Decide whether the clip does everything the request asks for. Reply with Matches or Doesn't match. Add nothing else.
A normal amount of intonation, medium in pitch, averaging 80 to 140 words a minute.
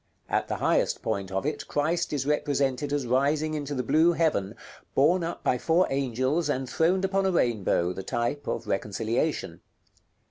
Doesn't match